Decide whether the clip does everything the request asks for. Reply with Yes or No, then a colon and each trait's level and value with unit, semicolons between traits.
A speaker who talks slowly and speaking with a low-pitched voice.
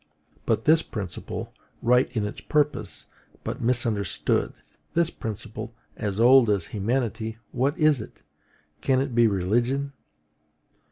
Yes: slow, 120 wpm; low, 120 Hz